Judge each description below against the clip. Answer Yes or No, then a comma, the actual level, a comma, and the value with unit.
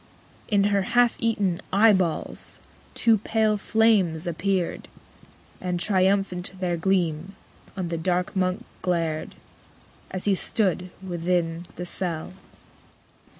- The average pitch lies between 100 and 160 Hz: No, medium, 185 Hz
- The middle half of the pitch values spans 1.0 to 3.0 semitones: Yes, narrow, 2.6 semitones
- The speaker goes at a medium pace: No, slow, 110 wpm